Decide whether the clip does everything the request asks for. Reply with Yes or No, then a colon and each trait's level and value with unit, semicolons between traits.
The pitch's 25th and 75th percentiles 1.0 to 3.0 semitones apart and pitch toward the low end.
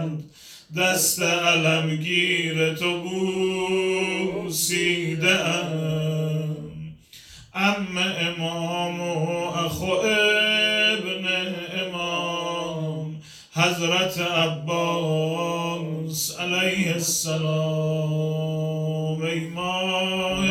No: narrow, 2.5 semitones; medium, 170 Hz